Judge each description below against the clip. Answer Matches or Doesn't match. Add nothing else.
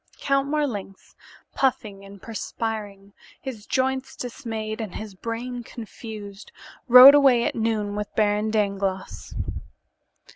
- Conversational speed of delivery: Doesn't match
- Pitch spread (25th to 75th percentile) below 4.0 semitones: Matches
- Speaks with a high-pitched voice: Matches